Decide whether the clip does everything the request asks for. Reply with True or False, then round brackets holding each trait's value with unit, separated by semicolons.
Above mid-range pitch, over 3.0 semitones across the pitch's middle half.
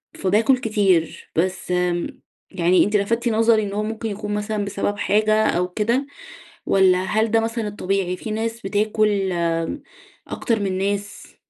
False (205 Hz; 2.5 semitones)